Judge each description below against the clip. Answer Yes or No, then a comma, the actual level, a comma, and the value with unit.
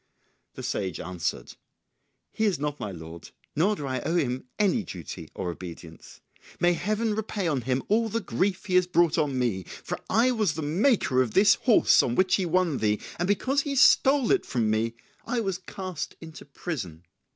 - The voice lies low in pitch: No, medium, 170 Hz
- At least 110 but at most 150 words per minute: No, average, 190 wpm